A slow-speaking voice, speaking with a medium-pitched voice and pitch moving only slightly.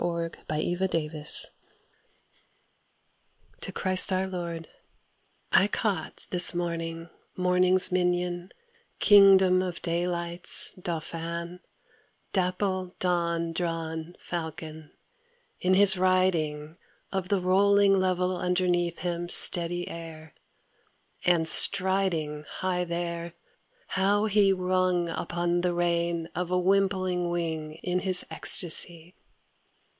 Yes: slow, 100 wpm; medium, 175 Hz; narrow, 1.7 semitones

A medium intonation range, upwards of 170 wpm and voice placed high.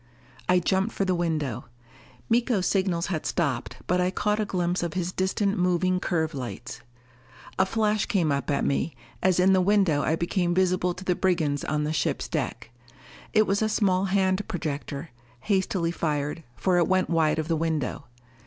No: average, 3.0 semitones; average, 180 wpm; medium, 180 Hz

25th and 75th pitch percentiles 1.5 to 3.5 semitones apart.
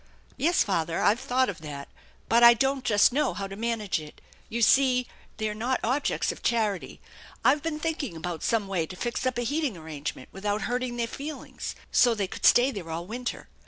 No: average, 4.8 semitones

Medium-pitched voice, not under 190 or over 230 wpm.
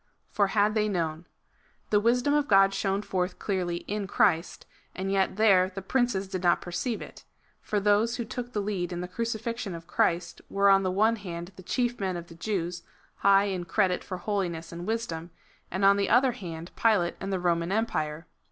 No: high, 195 Hz; average, 200 wpm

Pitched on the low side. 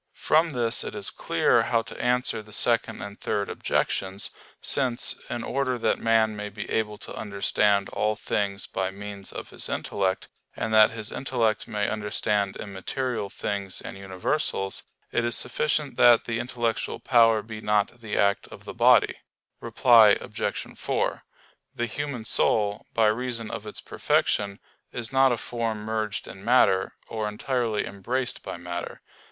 Yes: low, 110 Hz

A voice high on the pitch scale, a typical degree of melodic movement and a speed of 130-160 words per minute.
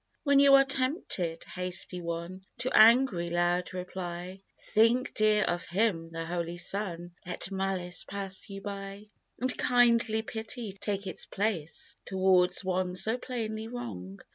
Yes: high, 195 Hz; average, 4.0 semitones; average, 140 wpm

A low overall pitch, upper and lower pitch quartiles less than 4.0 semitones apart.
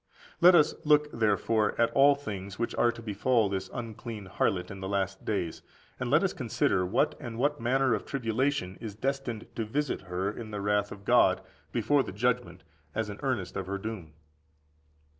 No: low, 110 Hz; average, 4.6 semitones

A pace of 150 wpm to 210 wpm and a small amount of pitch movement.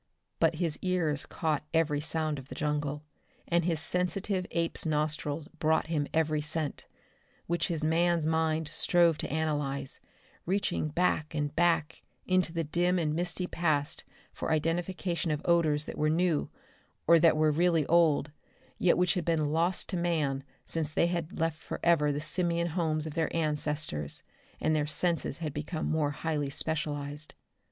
Yes: average, 160 wpm; narrow, 2.3 semitones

